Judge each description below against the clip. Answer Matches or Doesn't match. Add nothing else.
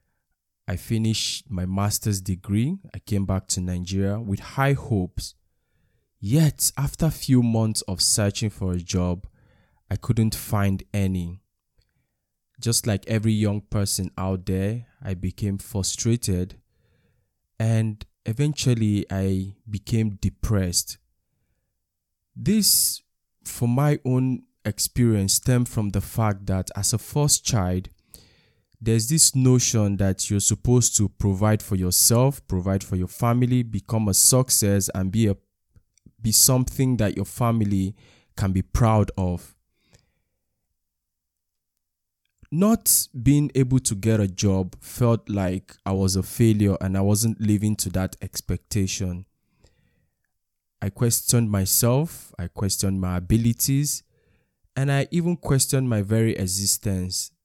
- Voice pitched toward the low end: Matches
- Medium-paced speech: Doesn't match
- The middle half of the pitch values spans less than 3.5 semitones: Doesn't match